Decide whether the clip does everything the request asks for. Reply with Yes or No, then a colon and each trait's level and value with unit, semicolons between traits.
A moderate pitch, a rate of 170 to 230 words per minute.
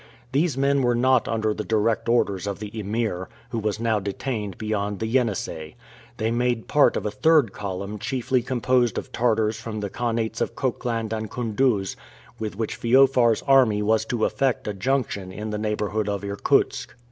No: low, 110 Hz; average, 175 wpm